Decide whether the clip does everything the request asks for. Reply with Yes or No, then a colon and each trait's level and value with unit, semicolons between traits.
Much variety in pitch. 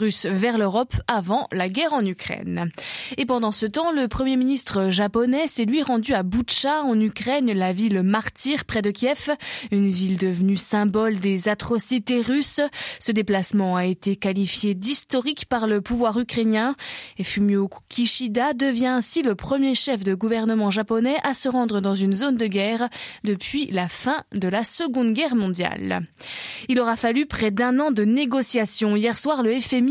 No: average, 4.2 semitones